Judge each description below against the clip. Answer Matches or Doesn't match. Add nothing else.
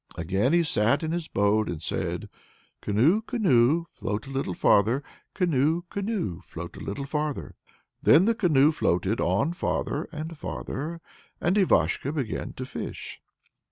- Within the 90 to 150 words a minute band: Matches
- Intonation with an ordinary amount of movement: Doesn't match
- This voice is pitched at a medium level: Matches